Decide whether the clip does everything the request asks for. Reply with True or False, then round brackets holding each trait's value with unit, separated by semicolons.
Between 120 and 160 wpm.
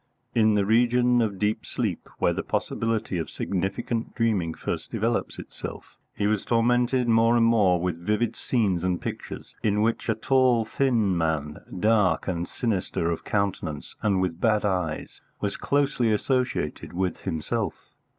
True (150 wpm)